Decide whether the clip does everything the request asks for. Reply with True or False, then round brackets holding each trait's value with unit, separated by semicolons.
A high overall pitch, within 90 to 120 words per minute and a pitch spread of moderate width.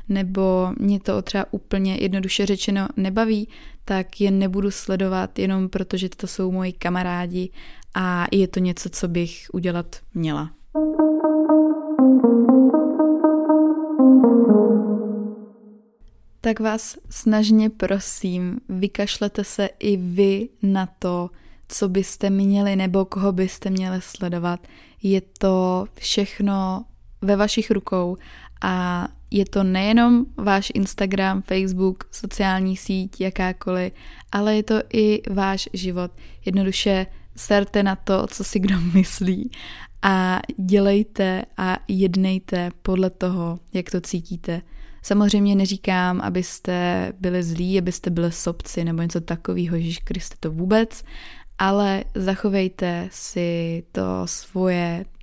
False (195 Hz; 115 wpm; 2.2 semitones)